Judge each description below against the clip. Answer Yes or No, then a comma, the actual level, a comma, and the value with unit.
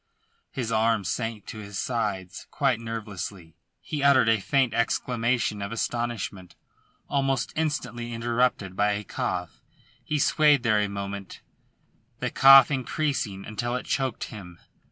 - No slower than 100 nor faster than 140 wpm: Yes, slow, 135 wpm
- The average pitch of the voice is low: Yes, low, 115 Hz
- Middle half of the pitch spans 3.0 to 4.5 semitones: Yes, average, 4.0 semitones